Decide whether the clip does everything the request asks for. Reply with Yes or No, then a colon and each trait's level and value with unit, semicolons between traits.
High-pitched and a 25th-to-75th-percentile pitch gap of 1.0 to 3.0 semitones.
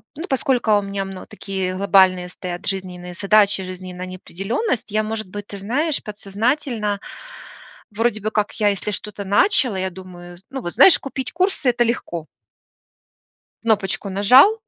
No: high, 205 Hz; average, 3.8 semitones